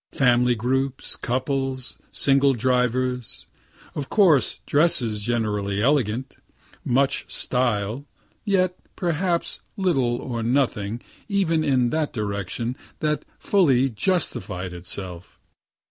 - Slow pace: Yes, slow, 95 wpm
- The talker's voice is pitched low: Yes, low, 130 Hz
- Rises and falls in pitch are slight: No, average, 4.2 semitones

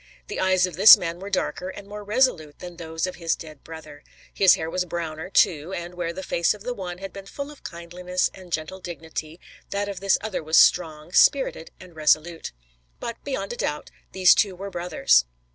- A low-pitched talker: No, medium, 180 Hz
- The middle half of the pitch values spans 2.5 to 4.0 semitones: Yes, average, 3.1 semitones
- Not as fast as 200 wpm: No, fast, 205 wpm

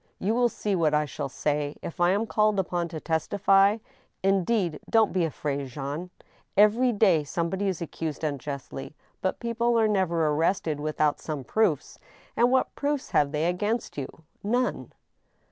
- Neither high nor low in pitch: Yes, medium, 175 Hz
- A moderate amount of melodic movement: No, wide, 5.8 semitones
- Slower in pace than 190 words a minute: Yes, average, 160 wpm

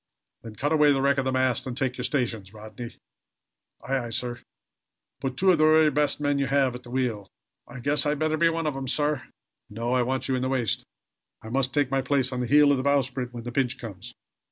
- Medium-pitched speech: No, low, 130 Hz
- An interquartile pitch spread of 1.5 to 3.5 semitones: Yes, average, 2.7 semitones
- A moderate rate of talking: No, fast, 245 wpm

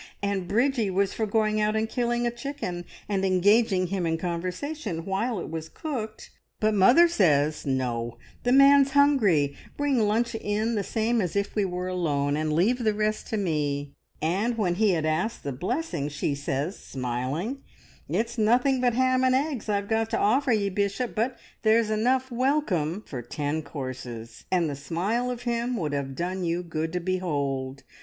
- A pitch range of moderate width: No, wide, 6.8 semitones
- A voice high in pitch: Yes, high, 200 Hz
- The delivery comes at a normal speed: Yes, average, 180 wpm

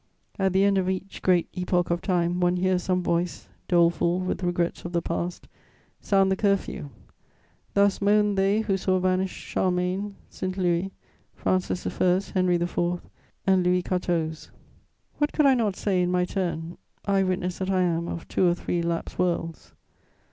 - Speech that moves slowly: No, average, 170 wpm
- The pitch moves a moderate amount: No, narrow, 1.6 semitones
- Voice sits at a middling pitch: Yes, medium, 180 Hz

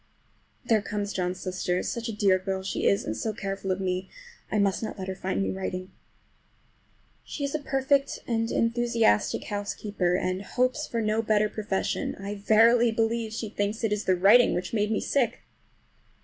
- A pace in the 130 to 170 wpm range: No, average, 185 wpm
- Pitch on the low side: No, high, 210 Hz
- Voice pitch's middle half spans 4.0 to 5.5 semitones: No, average, 3.2 semitones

